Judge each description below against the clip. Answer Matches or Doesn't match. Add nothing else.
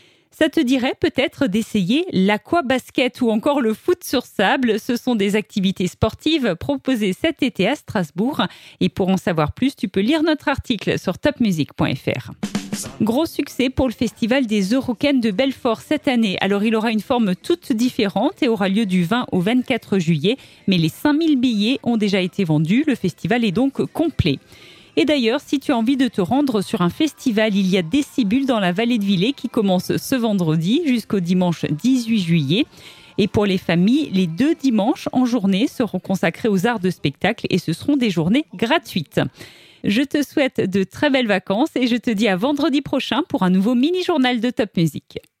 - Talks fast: Doesn't match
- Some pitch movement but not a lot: Doesn't match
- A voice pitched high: Matches